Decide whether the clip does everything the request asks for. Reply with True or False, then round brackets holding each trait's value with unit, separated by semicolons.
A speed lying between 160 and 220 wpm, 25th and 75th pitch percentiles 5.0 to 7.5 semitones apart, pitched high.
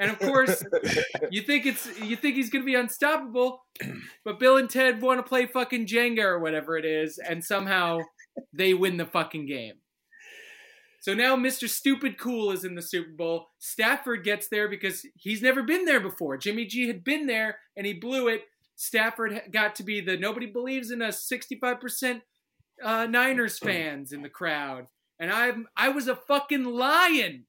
True (185 wpm; 5.3 semitones; 235 Hz)